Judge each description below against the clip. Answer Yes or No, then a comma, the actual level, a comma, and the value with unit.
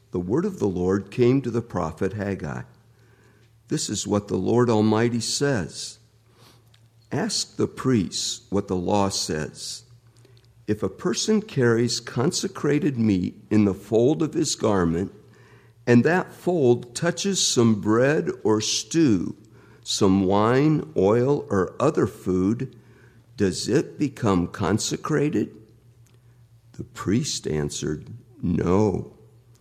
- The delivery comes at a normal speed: No, slow, 120 wpm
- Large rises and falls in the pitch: No, average, 3.0 semitones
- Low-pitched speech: Yes, low, 115 Hz